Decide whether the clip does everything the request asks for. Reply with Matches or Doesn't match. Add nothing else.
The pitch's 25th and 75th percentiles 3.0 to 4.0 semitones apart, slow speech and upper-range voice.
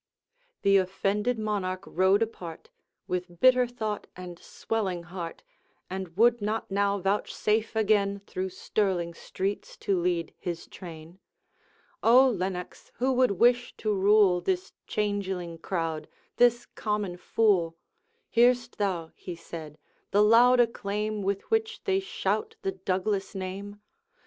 Matches